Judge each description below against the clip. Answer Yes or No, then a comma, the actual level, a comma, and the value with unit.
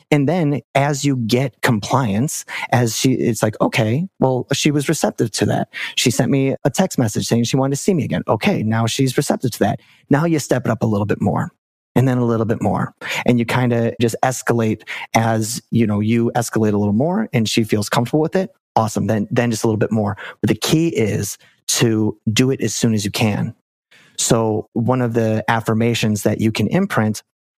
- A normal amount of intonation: Yes, average, 3.3 semitones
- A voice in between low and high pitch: No, low, 115 Hz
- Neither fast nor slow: No, fast, 215 wpm